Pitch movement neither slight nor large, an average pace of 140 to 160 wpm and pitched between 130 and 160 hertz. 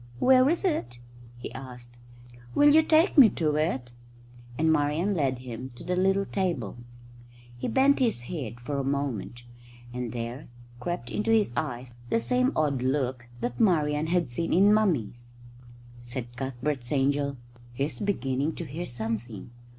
No: wide, 6.8 semitones; average, 150 wpm; medium, 140 Hz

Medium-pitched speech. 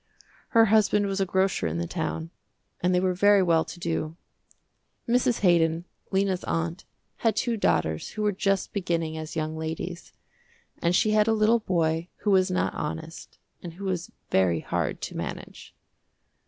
Yes: medium, 180 Hz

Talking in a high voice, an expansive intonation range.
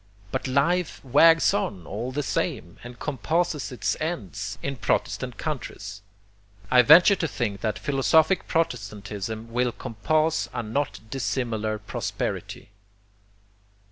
No: low, 125 Hz; wide, 6.2 semitones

